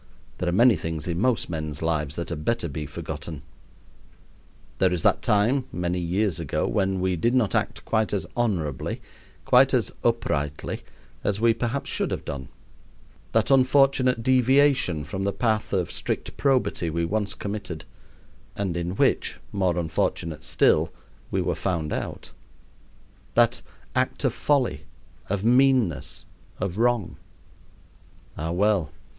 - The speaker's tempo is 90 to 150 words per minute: Yes, average, 140 wpm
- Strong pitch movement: Yes, wide, 6.0 semitones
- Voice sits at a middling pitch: No, very low, 95 Hz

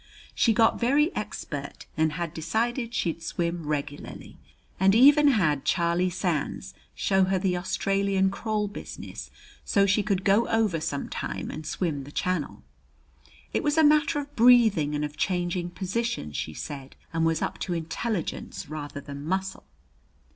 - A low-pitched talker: No, medium, 185 Hz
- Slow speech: No, average, 155 wpm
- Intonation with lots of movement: Yes, wide, 5.7 semitones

